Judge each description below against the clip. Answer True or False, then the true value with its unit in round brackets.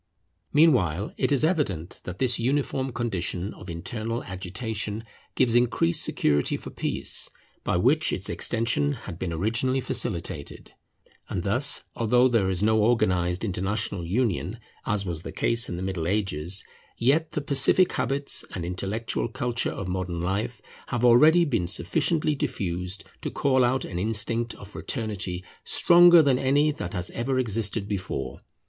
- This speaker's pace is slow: False (150 wpm)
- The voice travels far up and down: True (5.9 semitones)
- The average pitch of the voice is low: True (110 Hz)